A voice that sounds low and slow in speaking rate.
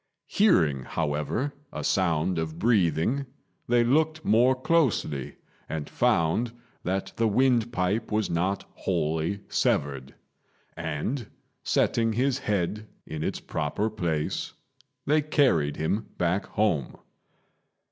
Yes: low, 100 Hz; slow, 105 wpm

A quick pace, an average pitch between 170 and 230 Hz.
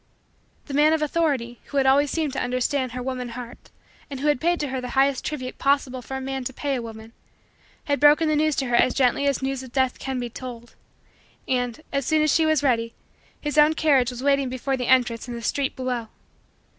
No: fast, 230 wpm; very high, 265 Hz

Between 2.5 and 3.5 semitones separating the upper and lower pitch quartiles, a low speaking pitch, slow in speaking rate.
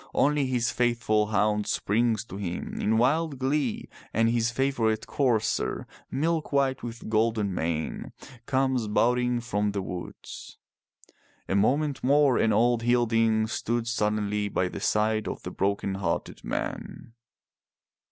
Yes: average, 3.0 semitones; low, 115 Hz; slow, 130 wpm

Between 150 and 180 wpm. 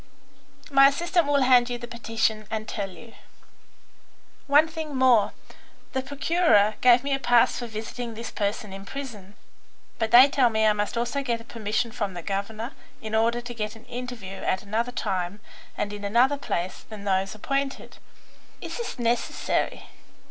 Yes: average, 170 wpm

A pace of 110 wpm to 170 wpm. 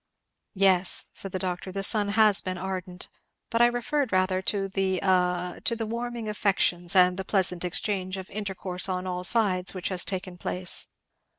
No: average, 180 wpm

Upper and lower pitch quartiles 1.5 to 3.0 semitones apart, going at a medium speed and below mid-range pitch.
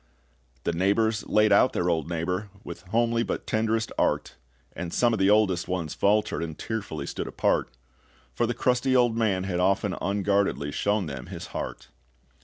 No: average, 4.1 semitones; average, 170 wpm; low, 100 Hz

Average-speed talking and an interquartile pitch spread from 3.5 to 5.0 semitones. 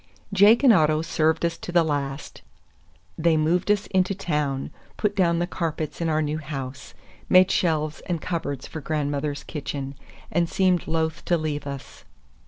No: average, 165 wpm; average, 2.9 semitones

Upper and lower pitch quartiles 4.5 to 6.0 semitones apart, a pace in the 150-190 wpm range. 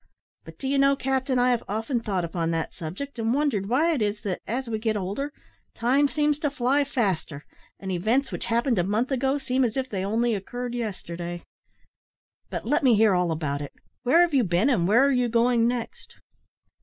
No: average, 5.3 semitones; fast, 205 wpm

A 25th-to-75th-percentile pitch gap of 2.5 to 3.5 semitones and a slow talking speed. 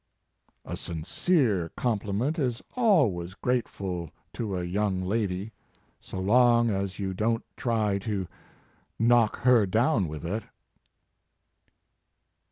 No: average, 4.2 semitones; slow, 115 wpm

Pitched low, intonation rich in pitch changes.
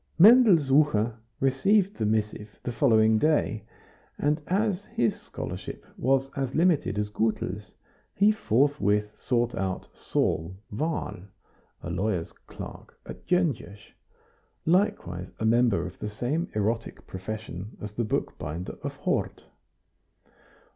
Yes: low, 115 Hz; wide, 6.3 semitones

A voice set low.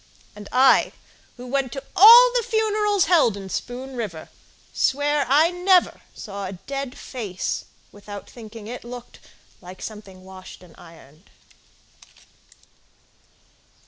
No: high, 245 Hz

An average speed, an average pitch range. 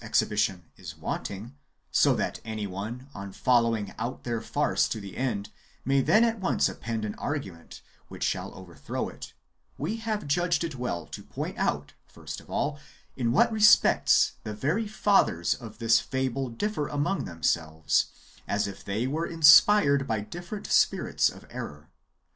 No: average, 160 wpm; wide, 6.9 semitones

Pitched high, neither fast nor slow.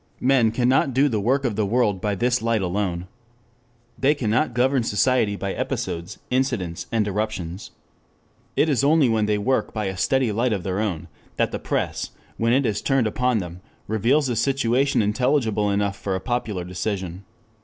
No: low, 110 Hz; average, 175 wpm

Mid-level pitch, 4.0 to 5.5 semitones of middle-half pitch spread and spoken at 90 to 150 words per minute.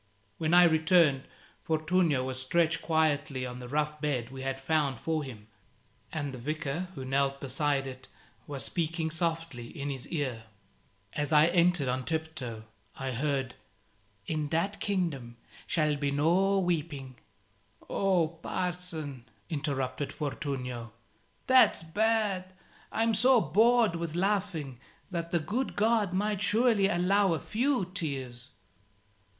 Yes: medium, 155 Hz; average, 5.0 semitones; slow, 135 wpm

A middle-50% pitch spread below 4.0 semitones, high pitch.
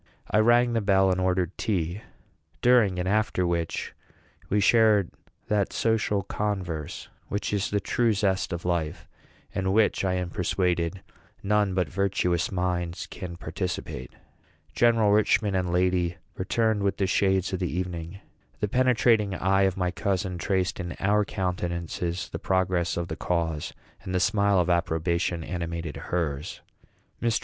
No: average, 2.7 semitones; very low, 95 Hz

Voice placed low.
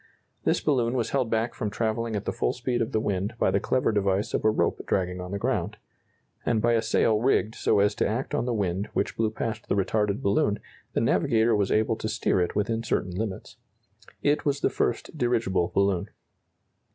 Yes: low, 110 Hz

